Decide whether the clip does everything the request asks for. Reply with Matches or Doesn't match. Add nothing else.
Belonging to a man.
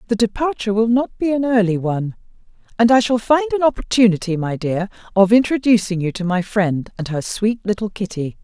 Doesn't match